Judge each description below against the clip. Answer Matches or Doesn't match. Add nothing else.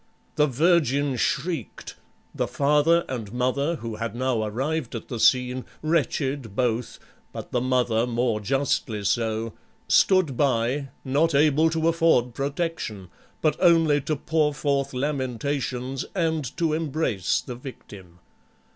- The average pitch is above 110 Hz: Matches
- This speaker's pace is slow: Matches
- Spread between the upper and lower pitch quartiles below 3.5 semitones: Doesn't match